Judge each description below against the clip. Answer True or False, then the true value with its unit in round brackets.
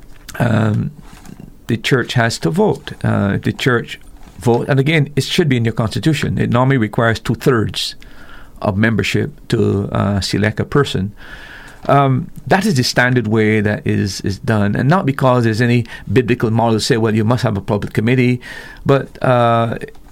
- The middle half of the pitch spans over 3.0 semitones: True (3.8 semitones)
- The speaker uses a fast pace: False (175 wpm)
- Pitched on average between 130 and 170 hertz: False (120 Hz)